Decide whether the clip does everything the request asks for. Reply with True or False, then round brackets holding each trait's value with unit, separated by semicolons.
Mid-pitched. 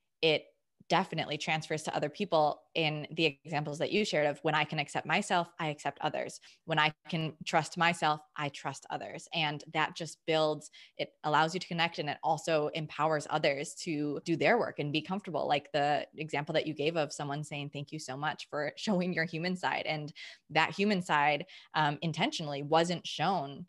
True (155 Hz)